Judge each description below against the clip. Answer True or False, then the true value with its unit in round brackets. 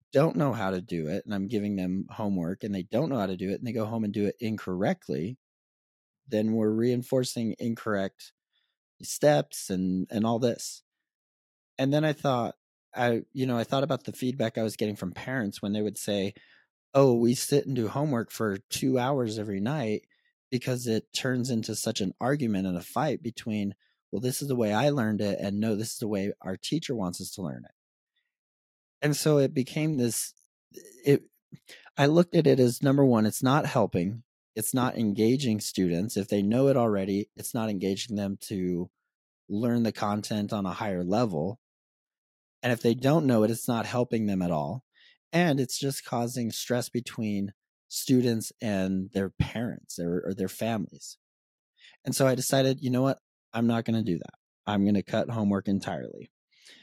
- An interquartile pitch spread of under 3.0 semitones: False (4.1 semitones)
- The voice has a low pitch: True (110 Hz)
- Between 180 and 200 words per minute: True (190 wpm)